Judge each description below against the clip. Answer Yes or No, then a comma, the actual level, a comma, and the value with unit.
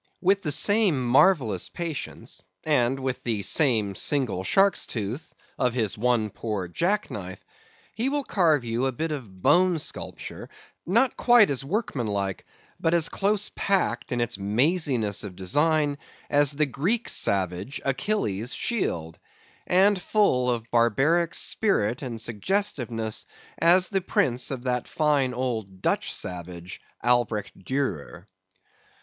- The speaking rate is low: Yes, slow, 130 wpm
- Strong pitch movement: Yes, wide, 7.6 semitones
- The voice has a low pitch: Yes, low, 130 Hz